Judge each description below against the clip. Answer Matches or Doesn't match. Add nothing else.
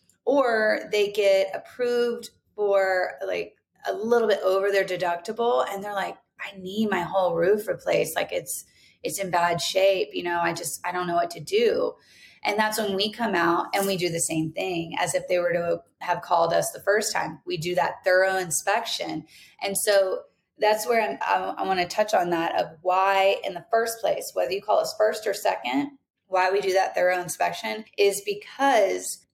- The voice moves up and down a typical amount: Matches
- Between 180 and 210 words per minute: Matches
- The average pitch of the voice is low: Doesn't match